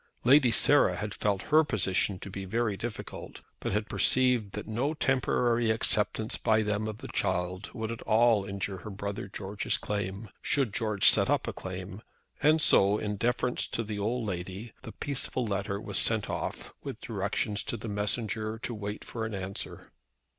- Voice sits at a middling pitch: No, low, 105 Hz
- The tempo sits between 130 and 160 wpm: No, average, 180 wpm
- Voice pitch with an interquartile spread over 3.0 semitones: No, average, 2.7 semitones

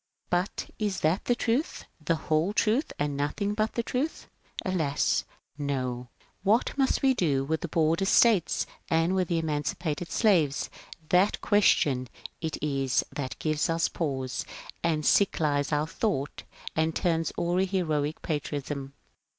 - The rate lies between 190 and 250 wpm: No, average, 160 wpm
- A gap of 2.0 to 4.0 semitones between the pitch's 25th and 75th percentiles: No, average, 4.7 semitones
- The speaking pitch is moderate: Yes, medium, 160 Hz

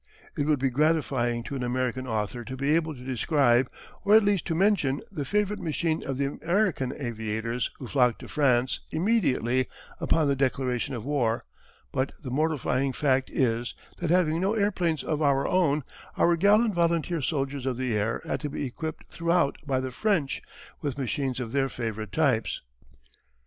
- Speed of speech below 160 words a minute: No, average, 175 wpm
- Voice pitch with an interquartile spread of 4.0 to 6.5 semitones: Yes, average, 4.4 semitones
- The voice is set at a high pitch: No, medium, 140 Hz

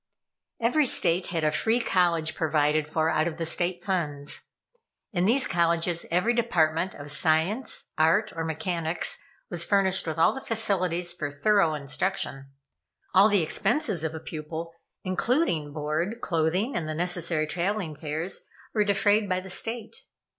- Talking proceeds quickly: No, average, 150 wpm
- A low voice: No, medium, 175 Hz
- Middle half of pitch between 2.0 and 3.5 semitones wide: No, average, 3.9 semitones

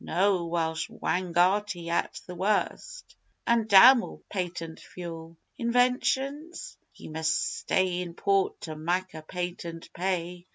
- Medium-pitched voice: Yes, medium, 180 Hz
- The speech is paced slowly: Yes, slow, 125 wpm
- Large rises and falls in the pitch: No, average, 3.6 semitones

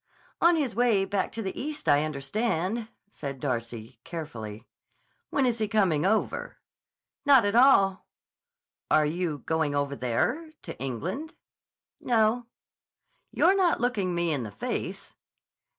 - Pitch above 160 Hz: Yes, high, 190 Hz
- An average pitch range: No, wide, 8.8 semitones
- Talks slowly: Yes, slow, 130 wpm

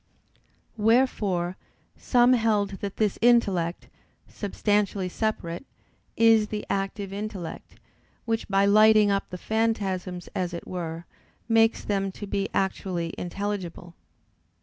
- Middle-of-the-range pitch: No, high, 200 Hz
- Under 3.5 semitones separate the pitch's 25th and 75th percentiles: Yes, average, 3.0 semitones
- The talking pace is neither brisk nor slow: No, slow, 110 wpm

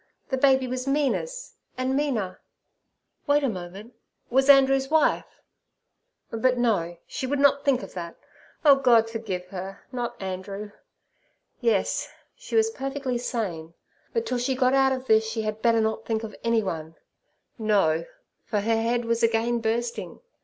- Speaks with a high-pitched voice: Yes, high, 235 Hz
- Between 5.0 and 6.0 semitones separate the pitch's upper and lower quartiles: No, average, 4.0 semitones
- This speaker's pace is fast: No, average, 145 wpm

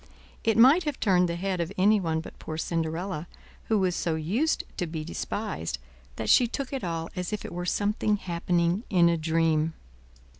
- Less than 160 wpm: No, average, 185 wpm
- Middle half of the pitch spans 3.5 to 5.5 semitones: Yes, average, 4.1 semitones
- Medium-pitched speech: Yes, medium, 175 Hz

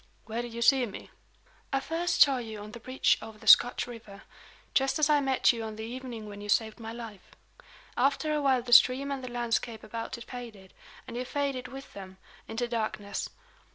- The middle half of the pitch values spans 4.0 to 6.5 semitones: No, average, 3.1 semitones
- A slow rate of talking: No, fast, 205 wpm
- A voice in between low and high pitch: No, high, 240 Hz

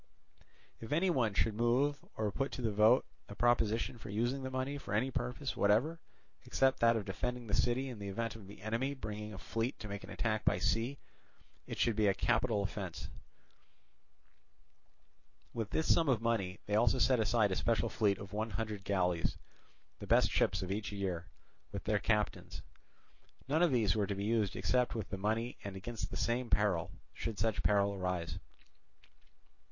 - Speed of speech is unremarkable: Yes, average, 185 wpm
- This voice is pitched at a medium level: No, low, 110 Hz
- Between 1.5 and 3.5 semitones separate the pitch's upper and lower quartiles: Yes, average, 3.1 semitones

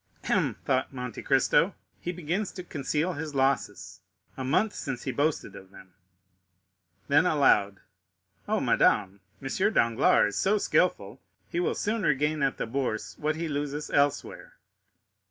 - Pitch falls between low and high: Yes, medium, 145 Hz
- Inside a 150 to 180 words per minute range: No, average, 140 wpm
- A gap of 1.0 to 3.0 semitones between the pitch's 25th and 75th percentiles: No, average, 4.5 semitones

